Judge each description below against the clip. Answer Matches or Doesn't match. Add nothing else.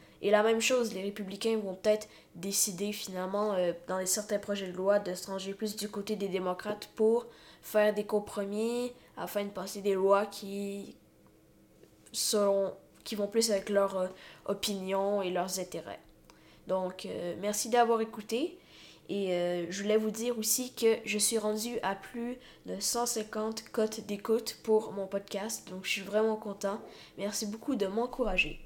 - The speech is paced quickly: Doesn't match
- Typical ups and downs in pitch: Doesn't match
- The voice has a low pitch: Doesn't match